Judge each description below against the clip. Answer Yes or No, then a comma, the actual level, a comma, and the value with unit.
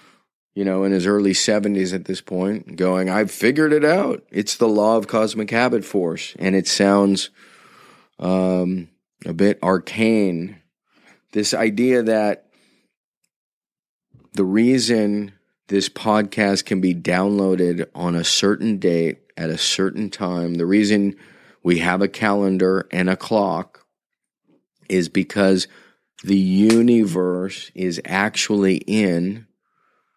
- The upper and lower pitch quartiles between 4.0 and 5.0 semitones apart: No, narrow, 2.4 semitones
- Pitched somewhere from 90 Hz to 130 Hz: Yes, low, 100 Hz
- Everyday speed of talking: No, slow, 125 wpm